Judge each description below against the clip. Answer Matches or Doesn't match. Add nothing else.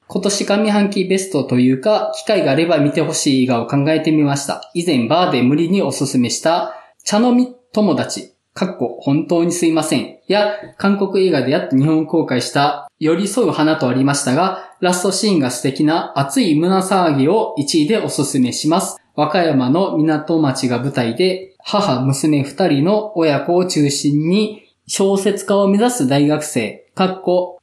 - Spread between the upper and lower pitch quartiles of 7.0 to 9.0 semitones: Doesn't match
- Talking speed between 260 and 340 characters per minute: Matches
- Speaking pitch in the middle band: Matches